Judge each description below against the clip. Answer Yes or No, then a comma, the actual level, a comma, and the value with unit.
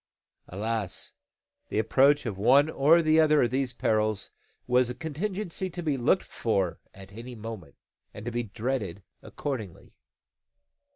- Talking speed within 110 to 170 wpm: Yes, average, 140 wpm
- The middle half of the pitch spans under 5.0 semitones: No, wide, 5.4 semitones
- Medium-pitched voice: No, low, 120 Hz